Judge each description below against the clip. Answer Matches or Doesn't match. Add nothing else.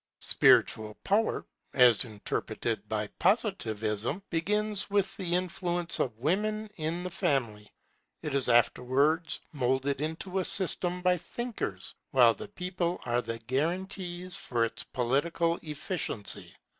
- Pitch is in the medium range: Matches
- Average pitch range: Doesn't match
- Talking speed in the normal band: Doesn't match